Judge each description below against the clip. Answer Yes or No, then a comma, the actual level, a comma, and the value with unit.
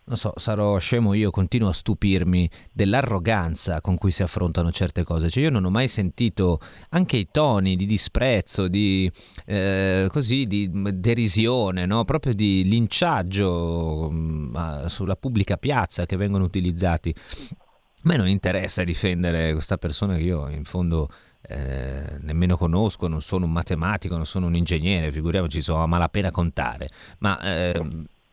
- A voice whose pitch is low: Yes, very low, 95 Hz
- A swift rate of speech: No, average, 150 wpm